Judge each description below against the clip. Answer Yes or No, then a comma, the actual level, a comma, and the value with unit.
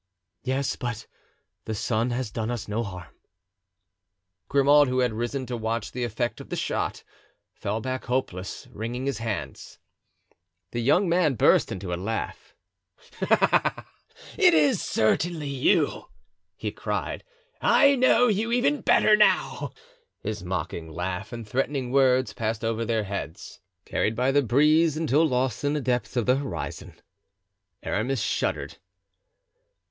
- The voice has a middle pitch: No, low, 125 Hz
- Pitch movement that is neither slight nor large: Yes, average, 4.4 semitones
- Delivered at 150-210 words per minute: No, average, 140 wpm